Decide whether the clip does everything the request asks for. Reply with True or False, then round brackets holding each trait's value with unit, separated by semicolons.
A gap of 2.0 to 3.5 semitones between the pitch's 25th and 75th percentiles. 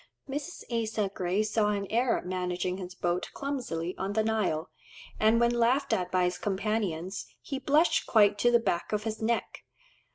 False (4.3 semitones)